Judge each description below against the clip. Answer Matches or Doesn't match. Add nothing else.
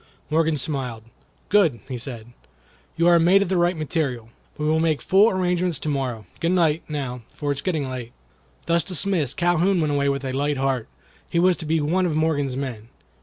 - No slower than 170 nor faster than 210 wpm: Matches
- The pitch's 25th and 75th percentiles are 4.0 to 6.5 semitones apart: Matches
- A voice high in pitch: Doesn't match